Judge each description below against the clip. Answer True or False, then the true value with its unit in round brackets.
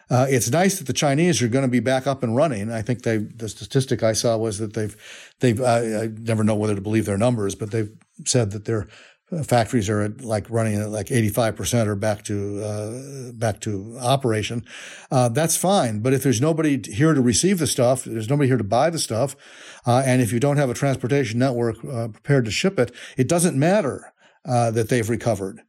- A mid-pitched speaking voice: False (120 Hz)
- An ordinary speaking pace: False (220 wpm)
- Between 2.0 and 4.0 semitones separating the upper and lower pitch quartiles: True (3.6 semitones)